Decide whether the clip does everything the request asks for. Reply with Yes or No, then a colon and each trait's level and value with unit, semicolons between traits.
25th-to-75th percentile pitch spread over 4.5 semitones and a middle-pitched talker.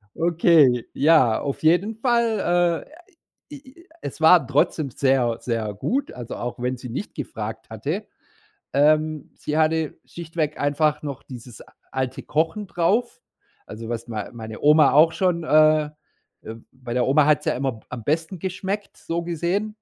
Yes: average, 5.3 semitones; medium, 155 Hz